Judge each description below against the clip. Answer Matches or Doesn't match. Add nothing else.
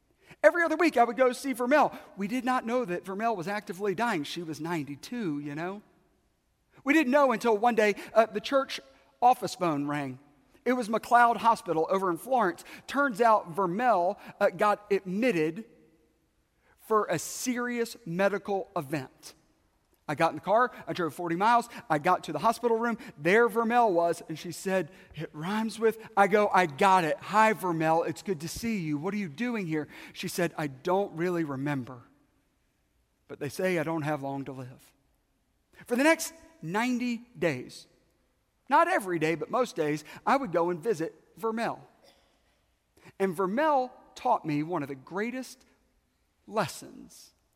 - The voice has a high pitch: Matches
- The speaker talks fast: Doesn't match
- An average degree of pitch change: Doesn't match